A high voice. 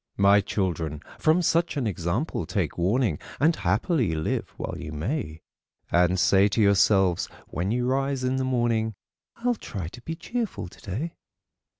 No: low, 105 Hz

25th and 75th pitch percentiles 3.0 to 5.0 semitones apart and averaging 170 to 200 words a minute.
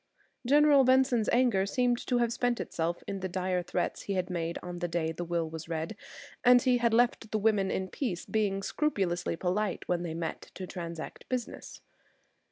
No: wide, 5.6 semitones; average, 180 wpm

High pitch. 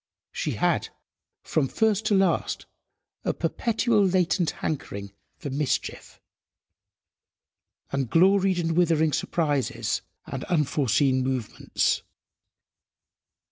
No: medium, 160 Hz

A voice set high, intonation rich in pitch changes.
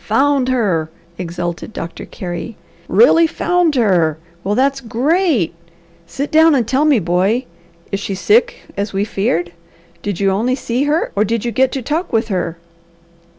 Yes: high, 230 Hz; wide, 6.4 semitones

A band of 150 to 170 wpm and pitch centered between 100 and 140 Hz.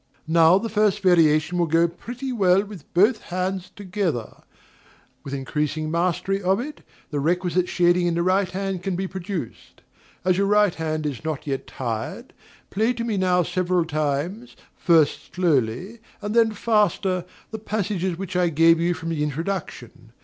No: average, 165 wpm; medium, 180 Hz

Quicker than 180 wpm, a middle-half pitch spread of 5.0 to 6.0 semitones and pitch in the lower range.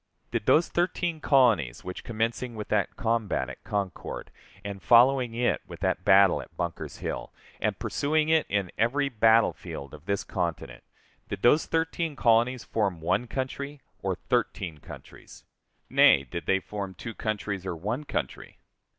No: average, 150 wpm; average, 5.3 semitones; low, 110 Hz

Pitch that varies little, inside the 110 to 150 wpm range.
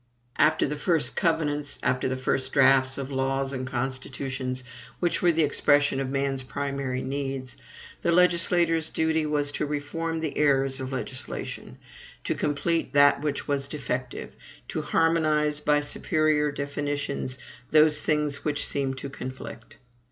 Yes: narrow, 2.3 semitones; average, 140 wpm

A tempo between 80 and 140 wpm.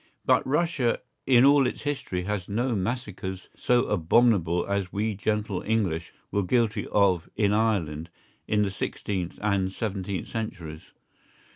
Yes: slow, 135 wpm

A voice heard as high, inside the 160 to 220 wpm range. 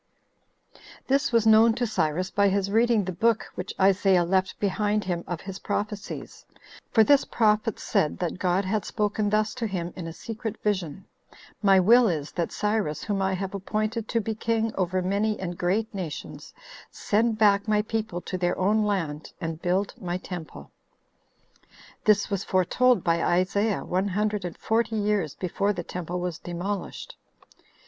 Yes: high, 200 Hz; average, 170 wpm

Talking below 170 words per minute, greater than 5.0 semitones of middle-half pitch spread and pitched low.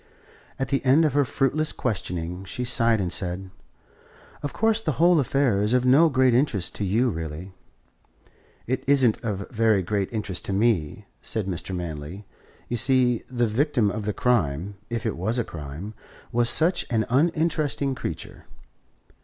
Yes: average, 160 wpm; wide, 5.6 semitones; low, 115 Hz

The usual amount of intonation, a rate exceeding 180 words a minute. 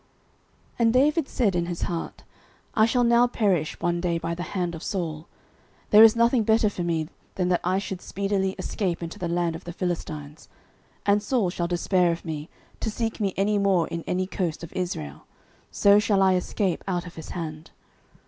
Yes: average, 3.4 semitones; average, 195 wpm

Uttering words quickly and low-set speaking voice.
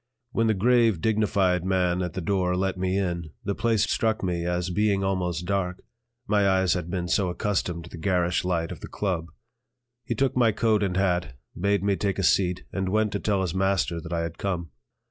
Yes: fast, 210 wpm; very low, 95 Hz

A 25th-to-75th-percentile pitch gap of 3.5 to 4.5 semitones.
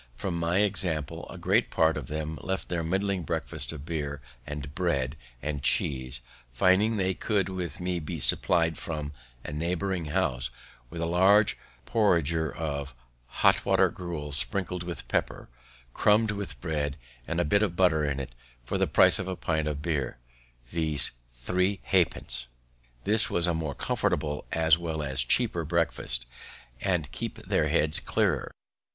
Yes: average, 3.9 semitones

